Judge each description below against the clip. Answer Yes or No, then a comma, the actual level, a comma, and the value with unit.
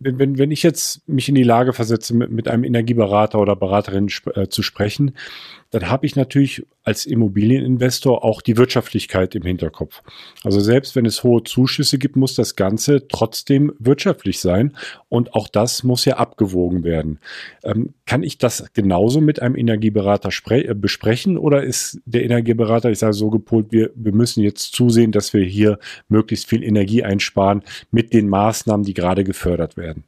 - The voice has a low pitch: Yes, low, 115 Hz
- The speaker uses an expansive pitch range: No, average, 3.7 semitones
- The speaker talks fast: No, average, 170 wpm